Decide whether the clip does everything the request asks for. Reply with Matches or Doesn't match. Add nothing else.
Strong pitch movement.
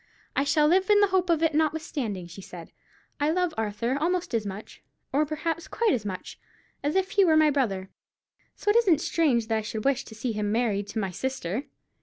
Matches